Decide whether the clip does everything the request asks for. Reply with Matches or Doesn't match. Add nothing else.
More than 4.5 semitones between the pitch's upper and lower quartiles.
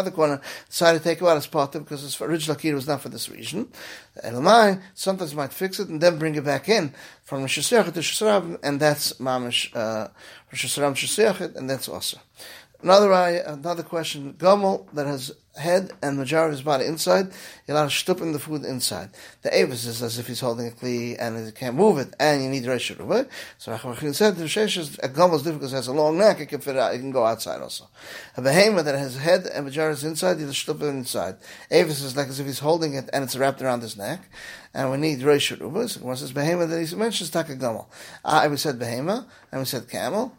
Doesn't match